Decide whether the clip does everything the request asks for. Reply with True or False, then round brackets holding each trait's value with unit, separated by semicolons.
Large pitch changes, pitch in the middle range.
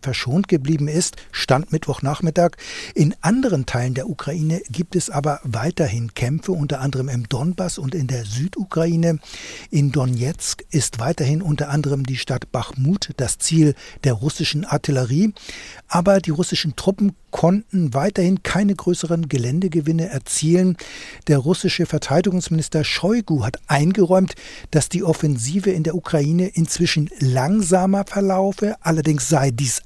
False (4.1 semitones; 160 Hz)